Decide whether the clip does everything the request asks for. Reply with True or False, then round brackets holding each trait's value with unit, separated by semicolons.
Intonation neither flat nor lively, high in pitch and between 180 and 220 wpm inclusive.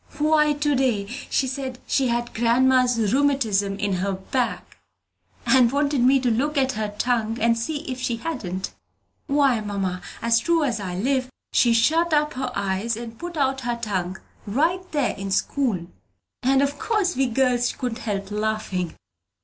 False (4.5 semitones; 245 Hz; 165 wpm)